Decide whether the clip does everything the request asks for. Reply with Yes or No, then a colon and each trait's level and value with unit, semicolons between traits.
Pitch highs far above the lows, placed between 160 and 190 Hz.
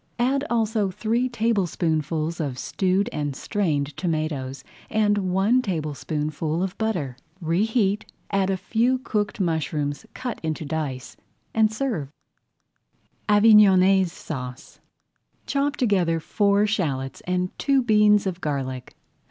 Yes: wide, 5.8 semitones; medium, 185 Hz